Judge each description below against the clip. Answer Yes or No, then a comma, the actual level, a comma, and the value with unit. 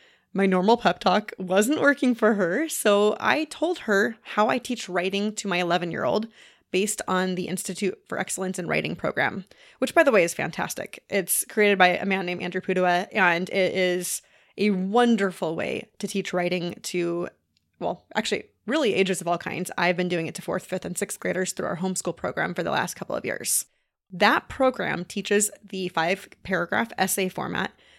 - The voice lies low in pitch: No, high, 190 Hz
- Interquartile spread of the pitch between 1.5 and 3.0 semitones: Yes, narrow, 2.5 semitones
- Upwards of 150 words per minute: Yes, average, 190 wpm